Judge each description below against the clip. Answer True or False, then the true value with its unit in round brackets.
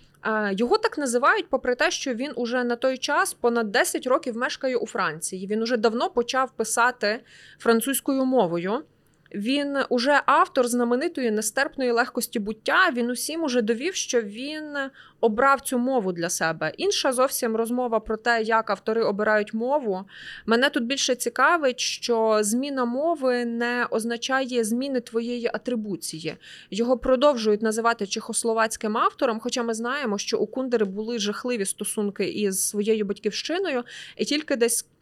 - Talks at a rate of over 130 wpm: True (140 wpm)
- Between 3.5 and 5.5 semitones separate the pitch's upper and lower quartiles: False (3.1 semitones)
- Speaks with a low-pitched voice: False (240 Hz)